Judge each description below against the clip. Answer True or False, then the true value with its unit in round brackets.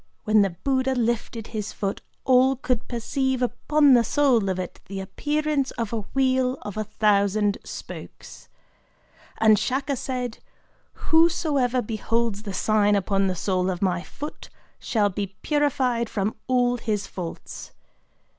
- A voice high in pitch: True (230 Hz)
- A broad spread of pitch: False (4.3 semitones)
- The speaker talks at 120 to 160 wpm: True (145 wpm)